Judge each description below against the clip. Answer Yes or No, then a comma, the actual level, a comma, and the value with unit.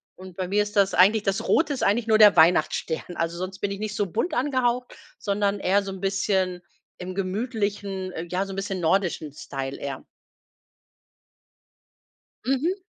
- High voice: Yes, high, 195 Hz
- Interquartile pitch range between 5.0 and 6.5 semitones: No, narrow, 2.5 semitones